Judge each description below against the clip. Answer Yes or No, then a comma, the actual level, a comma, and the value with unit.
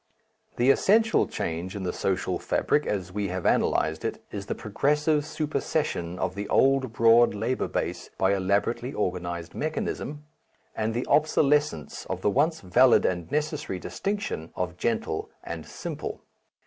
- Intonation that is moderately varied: No, wide, 8.2 semitones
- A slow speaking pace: No, average, 145 wpm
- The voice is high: No, low, 110 Hz